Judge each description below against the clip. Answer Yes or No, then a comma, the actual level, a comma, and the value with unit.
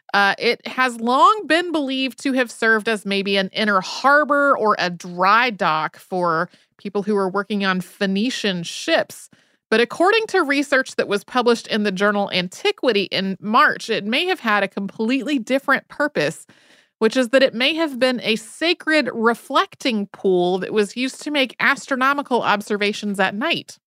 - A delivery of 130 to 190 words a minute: Yes, average, 170 wpm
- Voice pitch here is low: No, high, 230 Hz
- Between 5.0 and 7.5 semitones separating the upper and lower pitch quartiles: Yes, average, 5.3 semitones